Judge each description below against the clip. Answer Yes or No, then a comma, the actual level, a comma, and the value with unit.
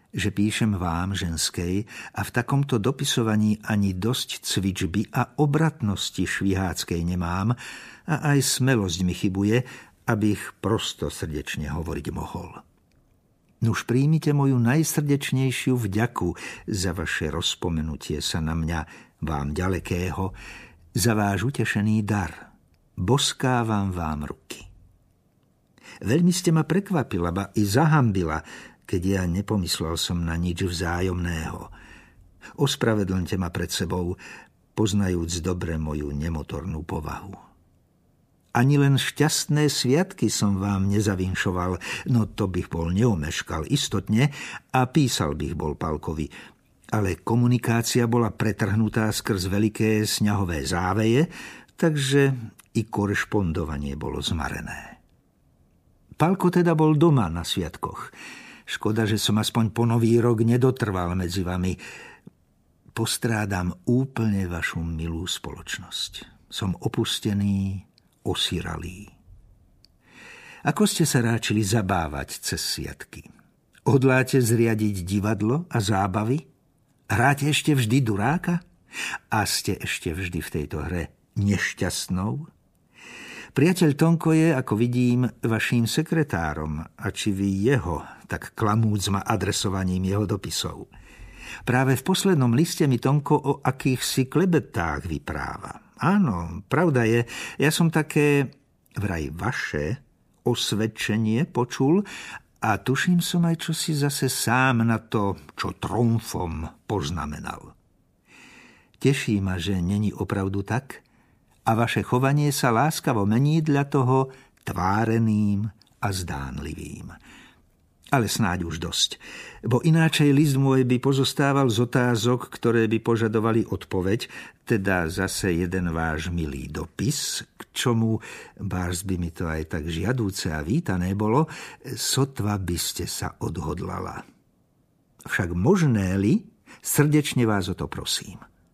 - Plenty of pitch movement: Yes, wide, 6.0 semitones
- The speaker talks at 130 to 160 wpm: No, average, 115 wpm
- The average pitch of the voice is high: No, low, 110 Hz